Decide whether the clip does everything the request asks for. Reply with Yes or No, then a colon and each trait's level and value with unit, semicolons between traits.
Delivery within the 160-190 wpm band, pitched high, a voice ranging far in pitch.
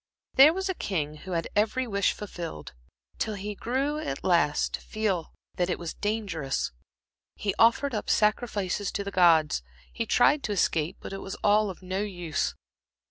No: average, 175 wpm; high, 200 Hz; average, 3.9 semitones